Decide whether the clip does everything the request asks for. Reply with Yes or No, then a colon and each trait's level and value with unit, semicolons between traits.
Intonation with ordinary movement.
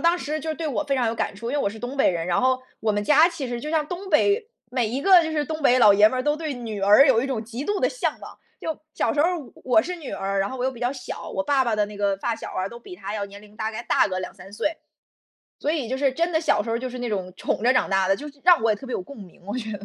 No: wide, 6.2 semitones